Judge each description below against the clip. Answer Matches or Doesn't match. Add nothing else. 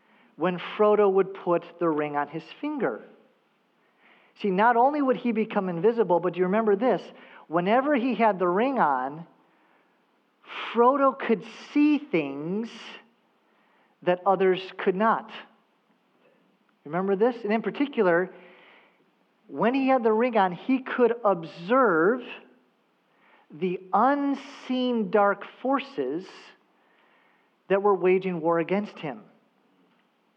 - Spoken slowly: Matches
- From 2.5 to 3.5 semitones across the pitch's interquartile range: Doesn't match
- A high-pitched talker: Matches